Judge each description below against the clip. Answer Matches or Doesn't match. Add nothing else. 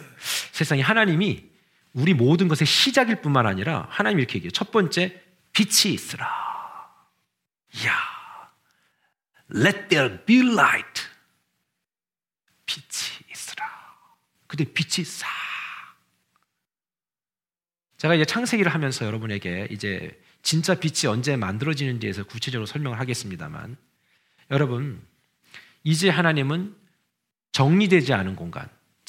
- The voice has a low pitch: Doesn't match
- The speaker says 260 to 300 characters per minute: Matches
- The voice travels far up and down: Matches